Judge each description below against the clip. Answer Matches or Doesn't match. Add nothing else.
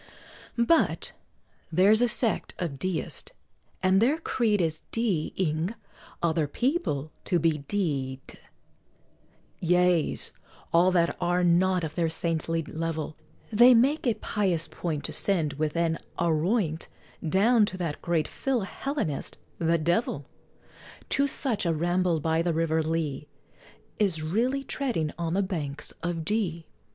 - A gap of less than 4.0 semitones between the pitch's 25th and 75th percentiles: Doesn't match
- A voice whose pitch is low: Doesn't match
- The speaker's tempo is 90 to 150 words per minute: Matches